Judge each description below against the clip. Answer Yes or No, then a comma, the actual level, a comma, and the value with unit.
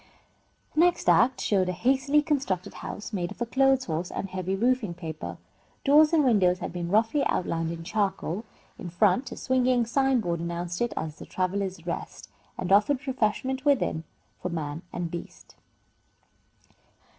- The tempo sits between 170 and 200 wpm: No, average, 160 wpm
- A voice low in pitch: No, high, 205 Hz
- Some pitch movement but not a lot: No, wide, 6.9 semitones